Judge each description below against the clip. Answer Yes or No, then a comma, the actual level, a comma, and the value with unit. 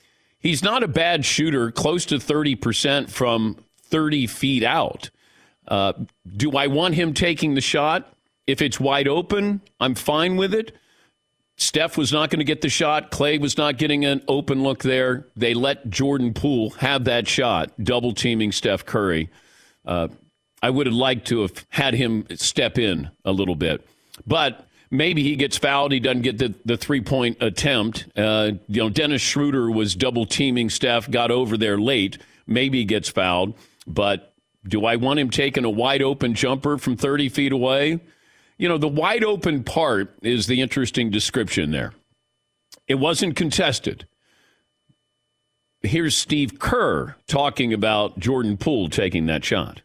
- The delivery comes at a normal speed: Yes, average, 160 wpm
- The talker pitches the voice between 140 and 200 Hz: No, low, 130 Hz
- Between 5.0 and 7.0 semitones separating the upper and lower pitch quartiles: No, average, 4.3 semitones